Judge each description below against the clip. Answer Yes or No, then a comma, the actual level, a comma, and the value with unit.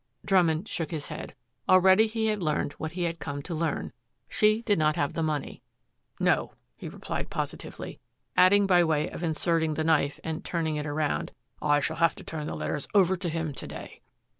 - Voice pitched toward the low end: No, medium, 160 Hz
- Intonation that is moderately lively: Yes, average, 3.2 semitones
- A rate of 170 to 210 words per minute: Yes, average, 195 wpm